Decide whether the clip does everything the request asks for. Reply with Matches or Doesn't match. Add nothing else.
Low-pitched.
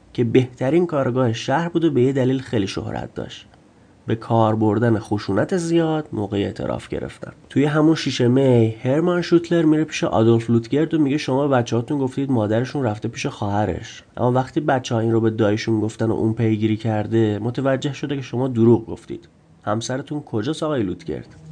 Matches